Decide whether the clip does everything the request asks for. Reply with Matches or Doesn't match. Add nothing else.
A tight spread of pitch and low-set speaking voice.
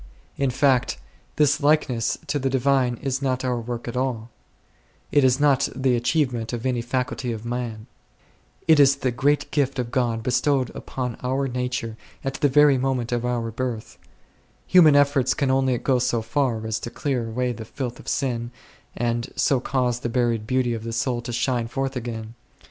Matches